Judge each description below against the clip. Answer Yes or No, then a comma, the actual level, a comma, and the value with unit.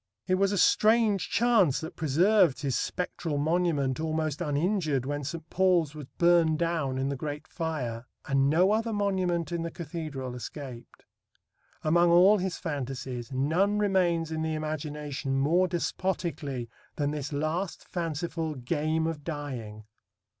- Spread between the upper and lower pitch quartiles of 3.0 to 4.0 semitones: Yes, average, 3.6 semitones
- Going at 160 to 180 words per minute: No, average, 140 wpm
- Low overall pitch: No, medium, 160 Hz